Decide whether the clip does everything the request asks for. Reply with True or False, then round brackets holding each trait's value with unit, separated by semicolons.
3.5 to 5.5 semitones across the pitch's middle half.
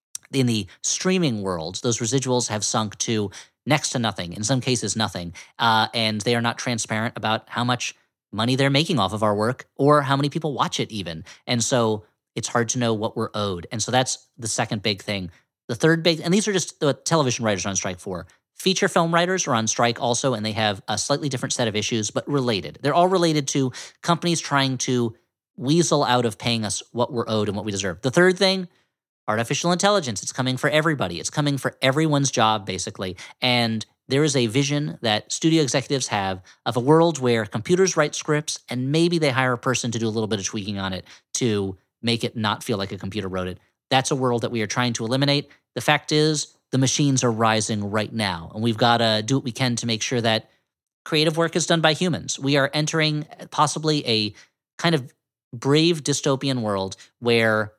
True (5.0 semitones)